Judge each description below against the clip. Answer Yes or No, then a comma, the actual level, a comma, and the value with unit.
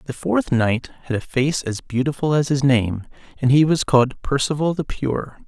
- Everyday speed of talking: Yes, average, 195 wpm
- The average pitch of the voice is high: No, low, 135 Hz